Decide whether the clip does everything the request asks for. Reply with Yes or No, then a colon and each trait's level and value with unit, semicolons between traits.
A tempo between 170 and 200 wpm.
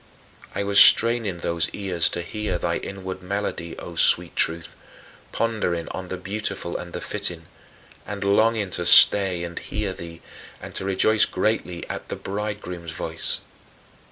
No: average, 150 wpm